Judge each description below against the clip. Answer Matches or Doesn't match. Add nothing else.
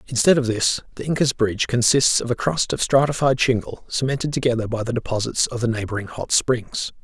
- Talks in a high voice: Doesn't match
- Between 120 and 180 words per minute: Doesn't match